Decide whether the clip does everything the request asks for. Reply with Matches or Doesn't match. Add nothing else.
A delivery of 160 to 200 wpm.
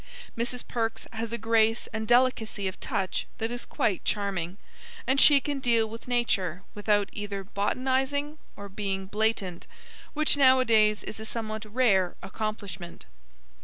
Doesn't match